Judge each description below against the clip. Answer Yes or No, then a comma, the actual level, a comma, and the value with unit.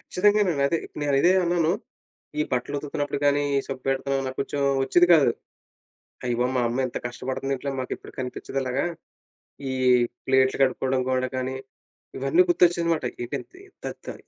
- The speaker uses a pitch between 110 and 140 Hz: Yes, low, 135 Hz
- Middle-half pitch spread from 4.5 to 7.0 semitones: No, average, 3.7 semitones